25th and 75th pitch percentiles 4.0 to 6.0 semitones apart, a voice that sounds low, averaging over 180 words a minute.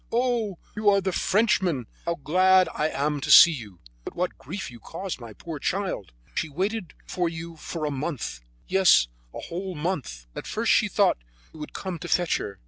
No: average, 4.5 semitones; medium, 170 Hz; average, 190 wpm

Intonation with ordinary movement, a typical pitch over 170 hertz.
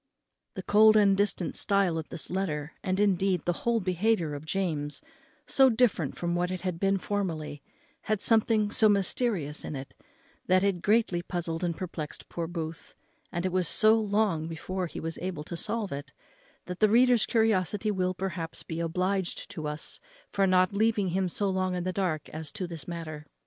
Yes: average, 3.6 semitones; medium, 185 Hz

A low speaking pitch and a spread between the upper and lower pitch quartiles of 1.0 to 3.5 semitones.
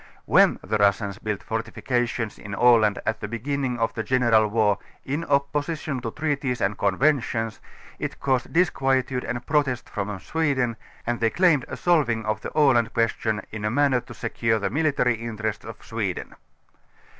No: low, 120 Hz; average, 3.9 semitones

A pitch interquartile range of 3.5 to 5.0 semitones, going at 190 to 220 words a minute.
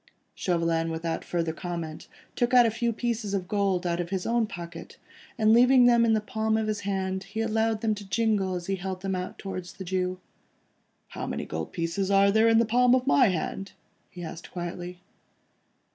Yes: average, 4.0 semitones; average, 195 wpm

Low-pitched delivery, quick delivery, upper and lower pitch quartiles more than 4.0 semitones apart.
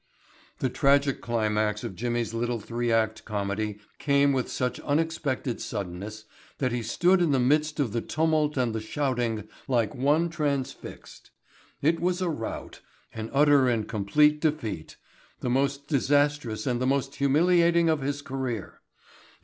No: low, 130 Hz; average, 150 wpm; average, 4.5 semitones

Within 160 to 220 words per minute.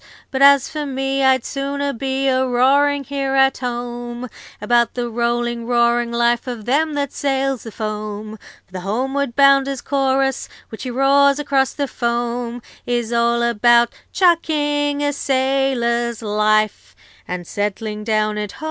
No: average, 150 wpm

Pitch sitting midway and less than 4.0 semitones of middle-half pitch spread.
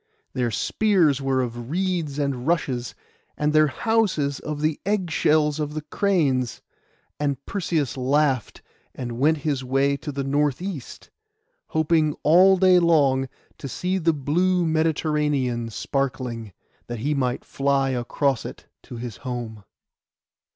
Yes: medium, 145 Hz; average, 3.6 semitones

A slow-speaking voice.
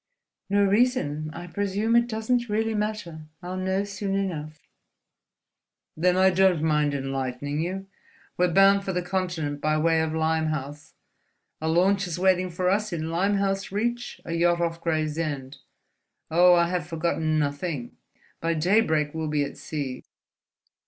No: average, 145 wpm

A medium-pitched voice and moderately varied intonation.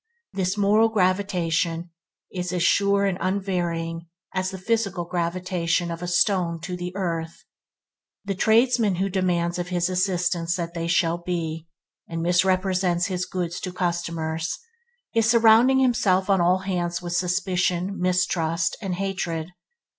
No: medium, 180 Hz; narrow, 2.0 semitones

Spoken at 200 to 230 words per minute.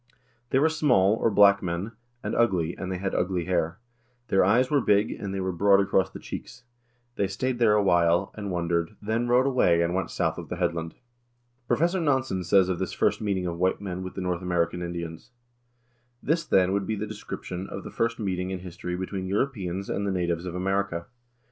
Yes: fast, 205 wpm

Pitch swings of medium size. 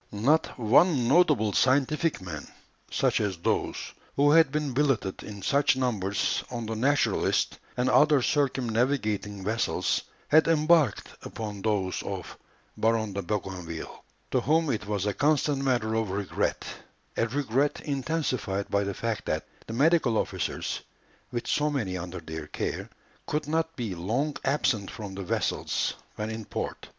No: wide, 6.0 semitones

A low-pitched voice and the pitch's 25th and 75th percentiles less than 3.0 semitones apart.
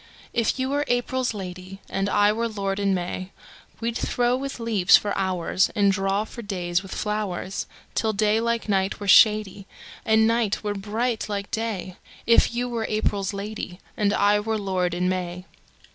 No: high, 205 Hz; narrow, 2.6 semitones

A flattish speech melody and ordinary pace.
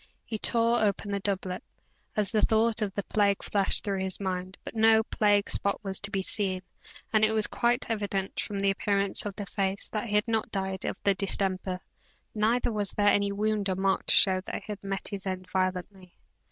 No: narrow, 1.9 semitones; fast, 210 wpm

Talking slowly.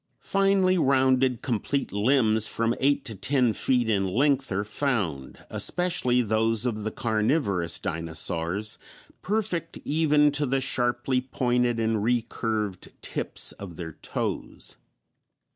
Yes: slow, 120 wpm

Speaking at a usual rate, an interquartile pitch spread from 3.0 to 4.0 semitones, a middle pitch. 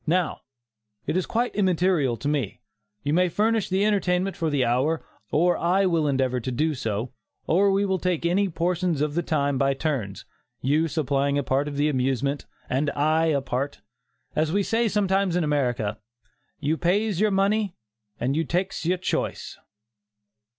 No: average, 170 wpm; average, 4.8 semitones; medium, 160 Hz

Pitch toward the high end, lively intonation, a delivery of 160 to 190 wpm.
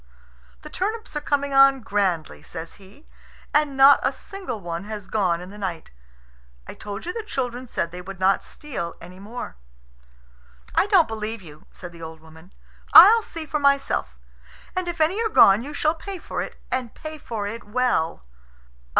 Yes: high, 230 Hz; wide, 8.3 semitones; average, 180 wpm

